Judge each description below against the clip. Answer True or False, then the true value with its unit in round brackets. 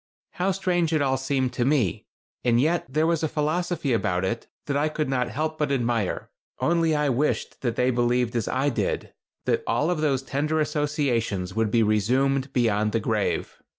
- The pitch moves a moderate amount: True (4.5 semitones)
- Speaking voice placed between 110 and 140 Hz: True (135 Hz)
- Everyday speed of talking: True (185 wpm)